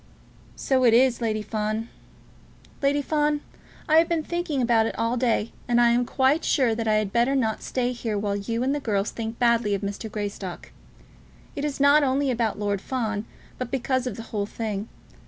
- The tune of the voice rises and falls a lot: No, average, 3.6 semitones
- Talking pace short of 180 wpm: No, average, 200 wpm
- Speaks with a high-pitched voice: Yes, high, 235 Hz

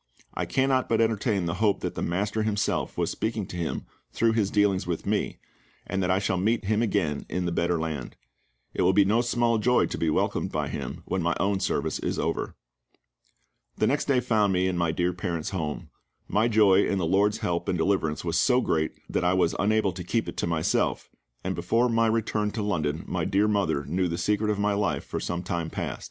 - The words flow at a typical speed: No, fast, 220 wpm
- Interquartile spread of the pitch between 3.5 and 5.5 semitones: Yes, average, 3.9 semitones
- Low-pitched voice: Yes, very low, 95 Hz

